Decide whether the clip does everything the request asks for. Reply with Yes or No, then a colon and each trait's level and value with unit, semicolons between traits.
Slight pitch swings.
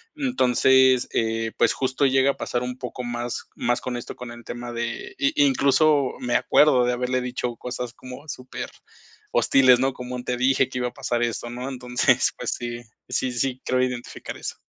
Yes: narrow, 1.4 semitones